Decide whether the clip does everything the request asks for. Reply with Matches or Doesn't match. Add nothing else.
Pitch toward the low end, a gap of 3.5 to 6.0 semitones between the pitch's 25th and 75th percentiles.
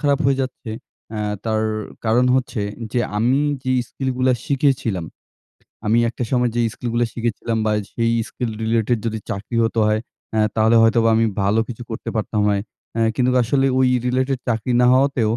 Doesn't match